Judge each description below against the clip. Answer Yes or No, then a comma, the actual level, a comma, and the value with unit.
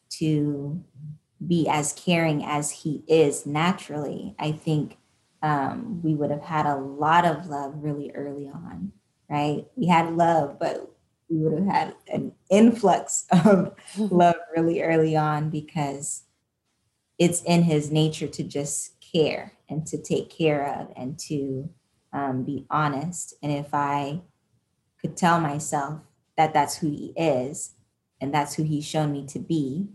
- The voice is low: No, medium, 150 Hz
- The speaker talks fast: No, average, 150 wpm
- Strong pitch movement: No, narrow, 2.5 semitones